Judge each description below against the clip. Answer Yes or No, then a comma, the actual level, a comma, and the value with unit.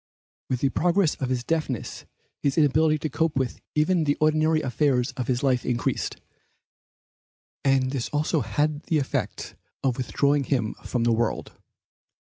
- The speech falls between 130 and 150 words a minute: Yes, average, 145 wpm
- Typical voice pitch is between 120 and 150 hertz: Yes, medium, 140 Hz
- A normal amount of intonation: Yes, average, 3.4 semitones